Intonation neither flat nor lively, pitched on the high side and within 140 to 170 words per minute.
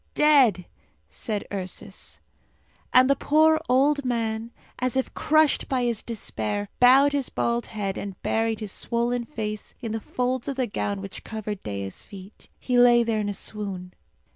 Yes: average, 3.9 semitones; high, 230 Hz; average, 165 wpm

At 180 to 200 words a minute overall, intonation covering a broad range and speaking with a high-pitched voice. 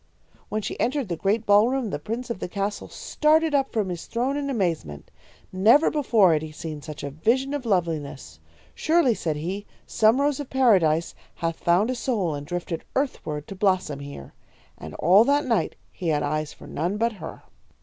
Yes: average, 190 wpm; wide, 7.8 semitones; high, 195 Hz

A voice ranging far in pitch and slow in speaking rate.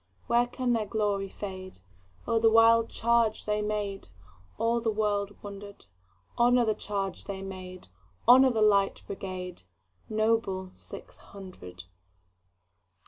No: average, 3.7 semitones; slow, 100 wpm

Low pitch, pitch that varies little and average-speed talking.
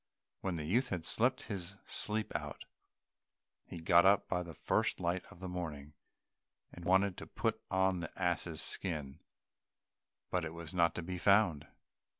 Yes: very low, 90 Hz; narrow, 2.3 semitones; average, 155 wpm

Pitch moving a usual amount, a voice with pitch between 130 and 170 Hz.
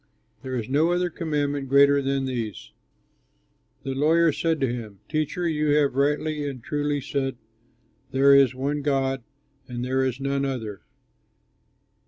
No: narrow, 2.0 semitones; medium, 140 Hz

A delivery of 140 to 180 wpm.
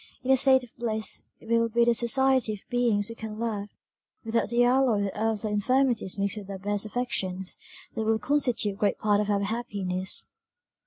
No: average, 190 wpm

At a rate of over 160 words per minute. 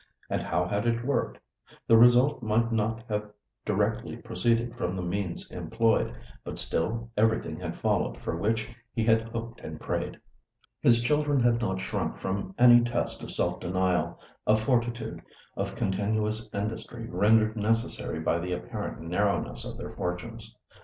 No: average, 155 wpm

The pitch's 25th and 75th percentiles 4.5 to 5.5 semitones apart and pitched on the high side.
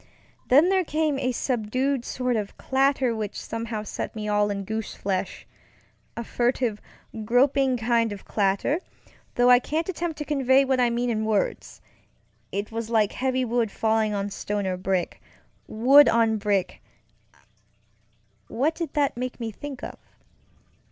No: average, 4.0 semitones; high, 235 Hz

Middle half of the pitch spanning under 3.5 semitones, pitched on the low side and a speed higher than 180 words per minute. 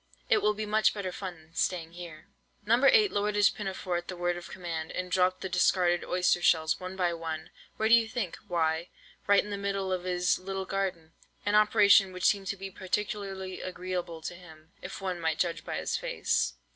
No: narrow, 2.4 semitones; medium, 185 Hz; average, 195 wpm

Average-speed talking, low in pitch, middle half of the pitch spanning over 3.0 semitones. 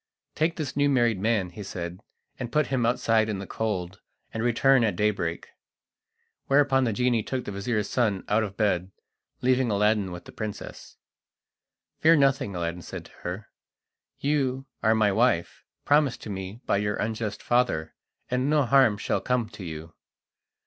Yes: average, 165 wpm; low, 110 Hz; average, 4.5 semitones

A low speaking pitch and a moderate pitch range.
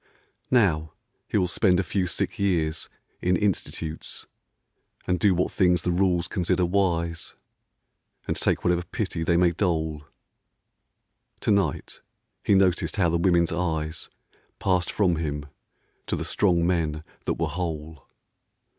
No: very low, 90 Hz; narrow, 2.2 semitones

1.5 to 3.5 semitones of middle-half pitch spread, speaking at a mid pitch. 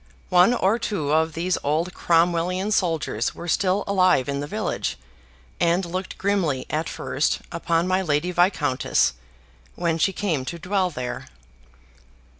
Yes: average, 2.9 semitones; medium, 170 Hz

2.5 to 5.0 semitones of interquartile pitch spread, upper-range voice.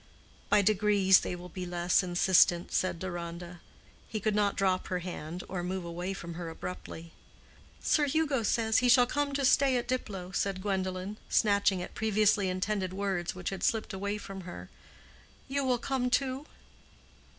Yes: average, 3.6 semitones; high, 195 Hz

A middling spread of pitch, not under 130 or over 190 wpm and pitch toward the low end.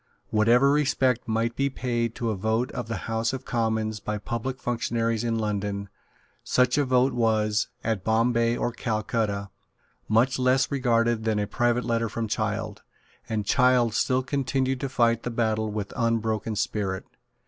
No: narrow, 2.3 semitones; average, 160 wpm; low, 115 Hz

